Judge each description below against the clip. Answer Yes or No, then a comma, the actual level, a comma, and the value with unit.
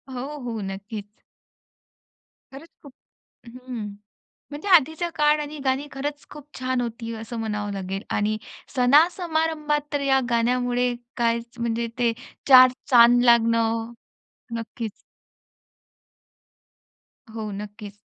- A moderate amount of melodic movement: Yes, average, 3.9 semitones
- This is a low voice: No, high, 245 Hz